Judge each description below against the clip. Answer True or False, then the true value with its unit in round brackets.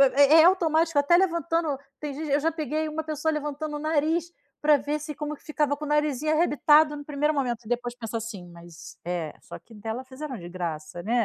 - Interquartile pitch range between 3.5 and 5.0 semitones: True (4.2 semitones)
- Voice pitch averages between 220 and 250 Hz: False (295 Hz)